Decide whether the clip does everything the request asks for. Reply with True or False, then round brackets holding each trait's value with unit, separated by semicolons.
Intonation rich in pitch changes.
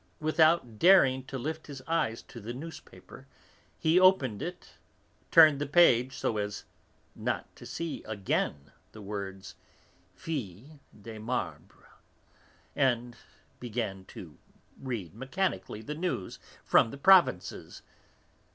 True (6.8 semitones)